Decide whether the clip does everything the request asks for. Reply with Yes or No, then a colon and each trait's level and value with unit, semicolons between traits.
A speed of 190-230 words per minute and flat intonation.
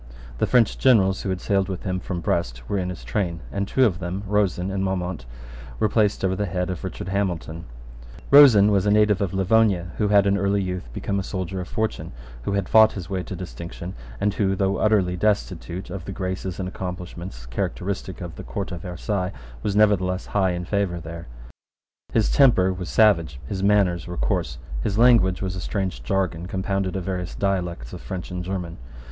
Yes: average, 200 wpm; narrow, 2.1 semitones